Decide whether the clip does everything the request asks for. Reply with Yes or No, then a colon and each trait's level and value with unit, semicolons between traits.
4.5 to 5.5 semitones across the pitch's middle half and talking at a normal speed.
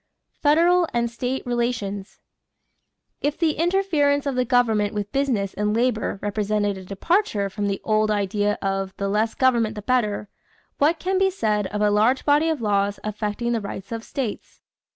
Yes: average, 4.9 semitones; average, 170 wpm